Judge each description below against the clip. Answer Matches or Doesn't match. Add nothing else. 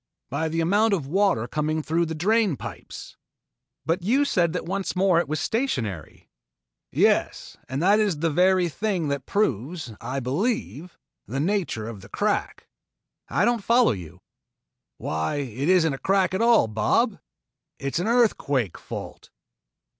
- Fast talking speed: Doesn't match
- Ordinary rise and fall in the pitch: Doesn't match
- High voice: Doesn't match